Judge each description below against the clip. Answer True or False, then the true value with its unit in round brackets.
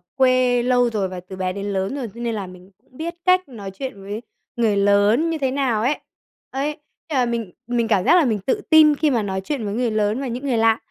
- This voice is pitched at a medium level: False (235 Hz)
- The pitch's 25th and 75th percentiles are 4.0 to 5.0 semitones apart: True (4.7 semitones)